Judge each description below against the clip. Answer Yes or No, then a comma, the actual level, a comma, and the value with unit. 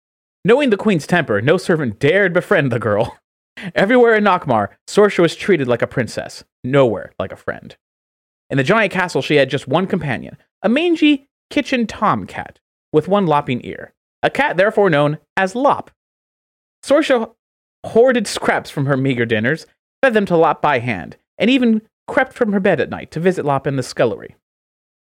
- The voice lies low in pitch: No, high, 190 Hz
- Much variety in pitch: Yes, wide, 8.0 semitones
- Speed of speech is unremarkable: Yes, average, 175 wpm